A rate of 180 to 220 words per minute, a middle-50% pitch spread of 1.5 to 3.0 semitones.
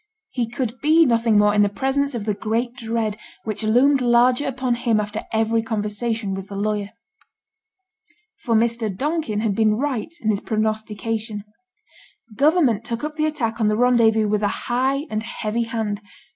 No: average, 170 wpm; average, 2.7 semitones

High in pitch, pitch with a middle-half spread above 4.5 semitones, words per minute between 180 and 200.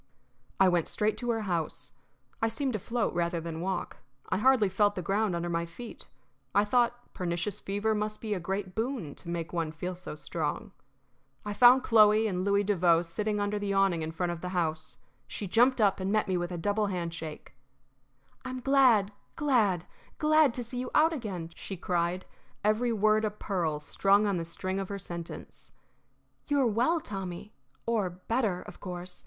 No: high, 200 Hz; average, 4.0 semitones; average, 185 wpm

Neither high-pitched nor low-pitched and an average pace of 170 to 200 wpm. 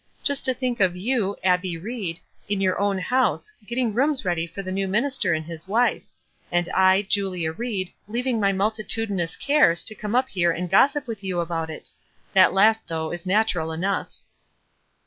No: high, 195 Hz; average, 185 wpm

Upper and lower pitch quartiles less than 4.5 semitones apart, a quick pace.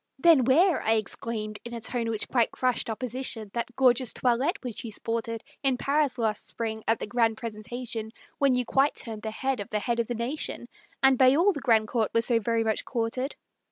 Yes: narrow, 2.5 semitones; fast, 210 wpm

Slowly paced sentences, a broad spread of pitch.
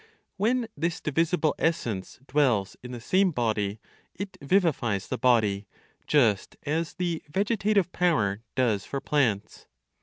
Yes: slow, 125 wpm; wide, 8.0 semitones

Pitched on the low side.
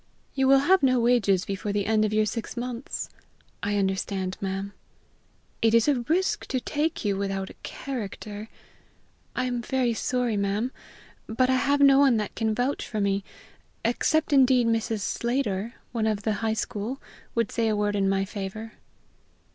No: high, 225 Hz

